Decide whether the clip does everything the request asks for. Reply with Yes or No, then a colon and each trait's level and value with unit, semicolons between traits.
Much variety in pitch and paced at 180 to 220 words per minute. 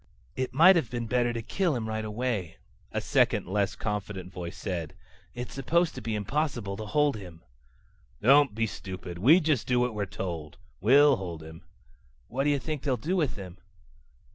Yes: wide, 6.3 semitones; average, 185 wpm